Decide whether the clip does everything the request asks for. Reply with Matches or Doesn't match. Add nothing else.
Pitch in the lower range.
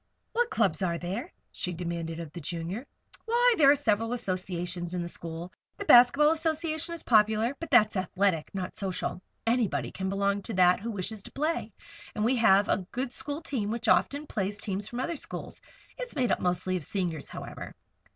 Doesn't match